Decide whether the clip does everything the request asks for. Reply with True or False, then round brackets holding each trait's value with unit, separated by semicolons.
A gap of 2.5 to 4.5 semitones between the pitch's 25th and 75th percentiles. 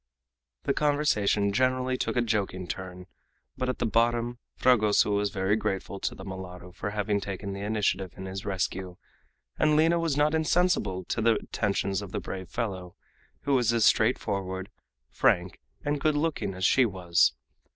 False (5.1 semitones)